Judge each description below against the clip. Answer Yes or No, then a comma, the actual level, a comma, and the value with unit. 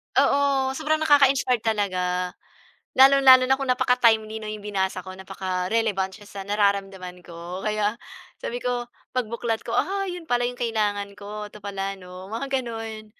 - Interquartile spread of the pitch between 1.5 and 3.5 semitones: No, average, 4.4 semitones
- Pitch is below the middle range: No, high, 215 Hz